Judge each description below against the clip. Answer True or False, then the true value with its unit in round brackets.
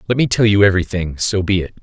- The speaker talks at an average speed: False (260 wpm)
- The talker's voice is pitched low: True (100 Hz)